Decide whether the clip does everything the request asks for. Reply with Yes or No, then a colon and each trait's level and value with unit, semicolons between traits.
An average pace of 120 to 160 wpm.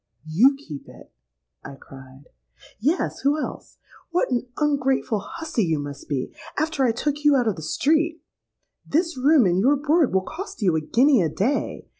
No: average, 170 wpm